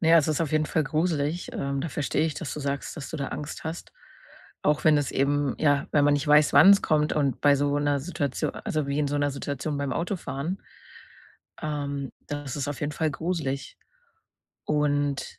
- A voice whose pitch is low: No, medium, 145 Hz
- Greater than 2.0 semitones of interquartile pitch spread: No, narrow, 1.6 semitones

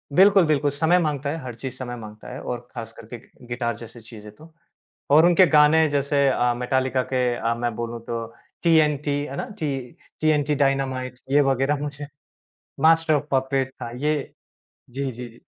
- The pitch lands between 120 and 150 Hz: Yes, low, 135 Hz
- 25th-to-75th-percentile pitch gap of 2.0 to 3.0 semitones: No, average, 3.6 semitones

